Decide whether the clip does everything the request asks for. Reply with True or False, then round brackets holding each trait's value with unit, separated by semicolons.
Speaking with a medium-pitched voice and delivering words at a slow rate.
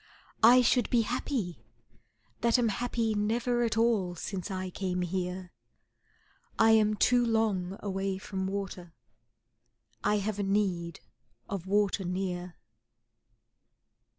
False (200 Hz; 120 wpm)